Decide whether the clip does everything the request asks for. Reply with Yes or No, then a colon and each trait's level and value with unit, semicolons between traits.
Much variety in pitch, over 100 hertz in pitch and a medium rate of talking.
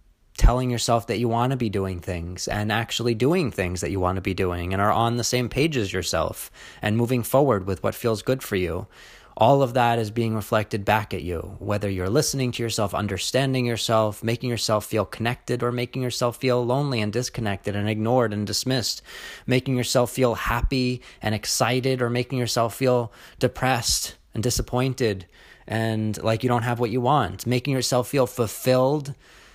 No: average, 3.3 semitones; low, 115 Hz; average, 185 wpm